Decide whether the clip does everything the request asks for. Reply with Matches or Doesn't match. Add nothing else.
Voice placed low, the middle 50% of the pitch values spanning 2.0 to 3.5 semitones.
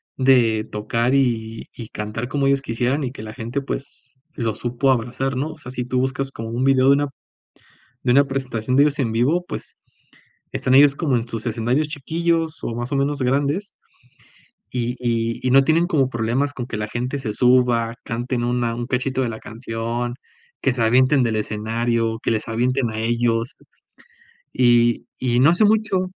Matches